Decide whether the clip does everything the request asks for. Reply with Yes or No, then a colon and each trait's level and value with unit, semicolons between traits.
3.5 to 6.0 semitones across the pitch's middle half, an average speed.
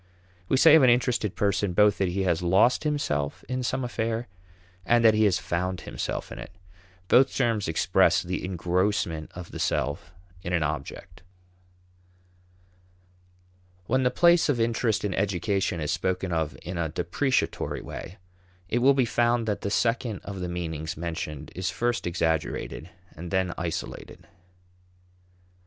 Yes: wide, 5.5 semitones; average, 150 wpm